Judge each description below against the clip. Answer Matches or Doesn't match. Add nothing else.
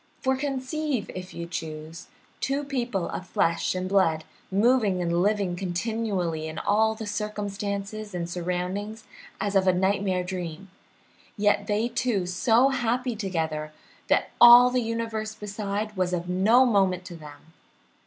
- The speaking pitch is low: Doesn't match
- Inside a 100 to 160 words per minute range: Matches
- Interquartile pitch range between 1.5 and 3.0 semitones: Doesn't match